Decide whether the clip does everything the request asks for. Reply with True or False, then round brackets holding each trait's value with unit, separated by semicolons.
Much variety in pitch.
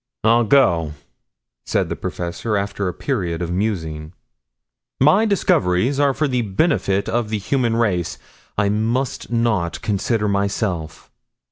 False (4.8 semitones)